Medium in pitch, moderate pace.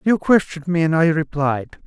Yes: medium, 165 Hz; average, 195 wpm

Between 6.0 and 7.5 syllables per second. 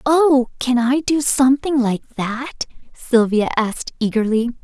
No: 4.0 syllables/s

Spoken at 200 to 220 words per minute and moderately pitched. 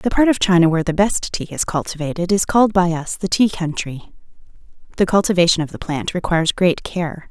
Yes: fast, 205 wpm; medium, 175 Hz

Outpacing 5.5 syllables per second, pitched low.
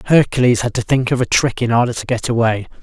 Yes: 6.4 syllables/s; low, 120 Hz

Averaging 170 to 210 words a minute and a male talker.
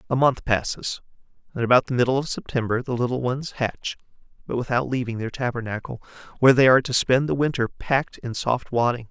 Yes: average, 190 wpm; male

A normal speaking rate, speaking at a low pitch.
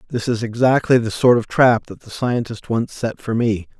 No: fast, 220 wpm; low, 115 Hz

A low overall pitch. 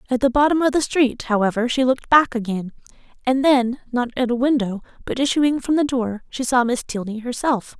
No: very high, 250 Hz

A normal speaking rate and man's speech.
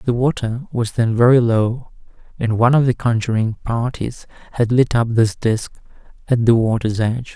Yes: average, 170 wpm; male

